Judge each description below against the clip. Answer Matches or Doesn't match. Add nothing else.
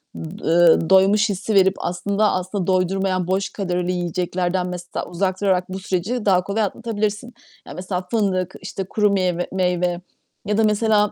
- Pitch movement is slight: Matches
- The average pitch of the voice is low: Doesn't match